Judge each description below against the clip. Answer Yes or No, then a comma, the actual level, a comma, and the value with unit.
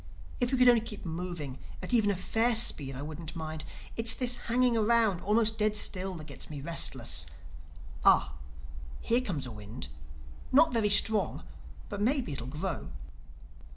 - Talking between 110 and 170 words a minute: Yes, average, 150 wpm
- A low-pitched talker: No, high, 190 Hz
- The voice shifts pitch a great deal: Yes, wide, 8.1 semitones